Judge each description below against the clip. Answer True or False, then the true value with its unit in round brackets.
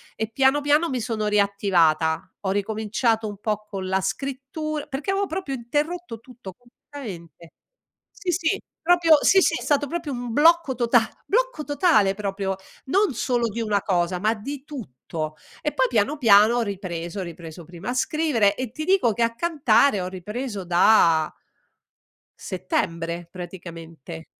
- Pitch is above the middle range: True (225 Hz)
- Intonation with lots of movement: True (7.2 semitones)